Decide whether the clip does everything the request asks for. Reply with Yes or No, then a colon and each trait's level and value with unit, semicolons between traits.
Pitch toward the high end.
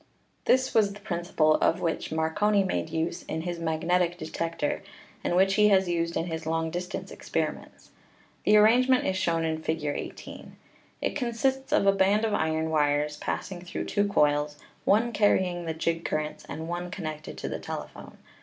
No: medium, 175 Hz